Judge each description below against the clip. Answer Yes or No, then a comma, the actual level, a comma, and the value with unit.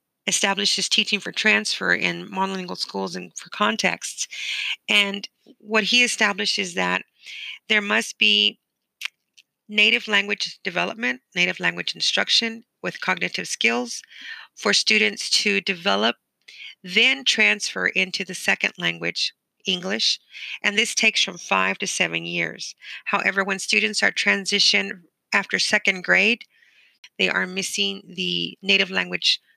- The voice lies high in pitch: Yes, high, 200 Hz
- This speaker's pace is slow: Yes, slow, 125 wpm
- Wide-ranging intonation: No, average, 2.7 semitones